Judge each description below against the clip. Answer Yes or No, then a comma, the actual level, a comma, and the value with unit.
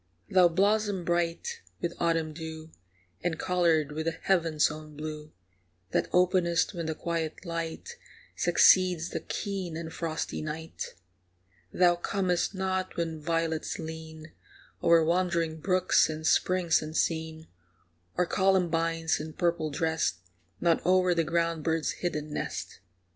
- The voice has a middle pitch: Yes, medium, 165 Hz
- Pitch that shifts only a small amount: Yes, narrow, 2.0 semitones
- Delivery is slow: Yes, slow, 125 wpm